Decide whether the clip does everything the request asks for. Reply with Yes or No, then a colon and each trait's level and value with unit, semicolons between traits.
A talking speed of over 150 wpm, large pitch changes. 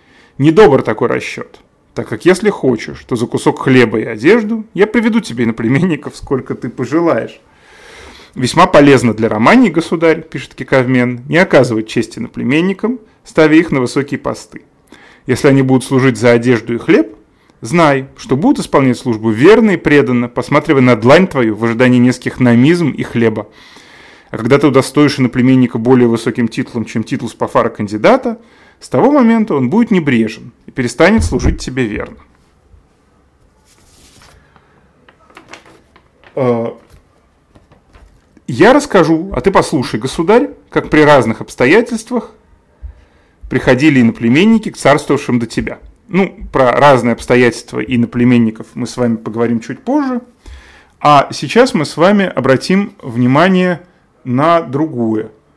No: average, 135 wpm; wide, 6.0 semitones